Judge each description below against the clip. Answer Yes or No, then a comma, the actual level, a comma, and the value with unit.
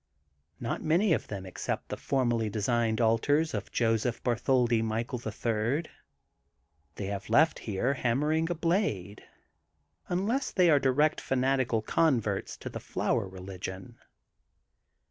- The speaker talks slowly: Yes, slow, 130 wpm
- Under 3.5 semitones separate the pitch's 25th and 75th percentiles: No, wide, 5.5 semitones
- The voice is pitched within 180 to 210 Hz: No, low, 120 Hz